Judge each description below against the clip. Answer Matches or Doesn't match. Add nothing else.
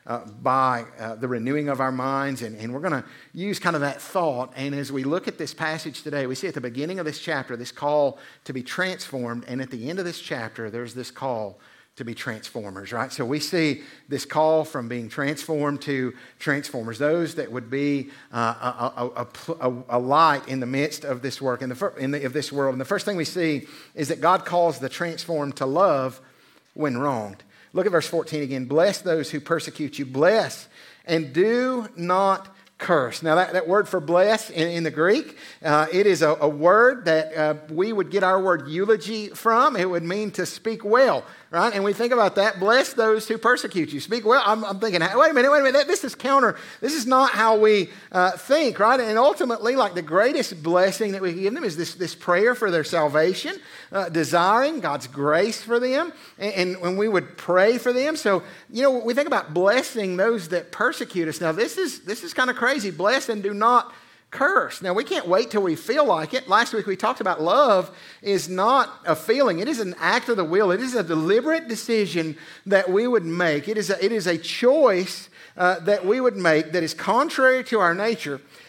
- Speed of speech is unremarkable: Doesn't match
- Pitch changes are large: Matches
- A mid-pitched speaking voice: Matches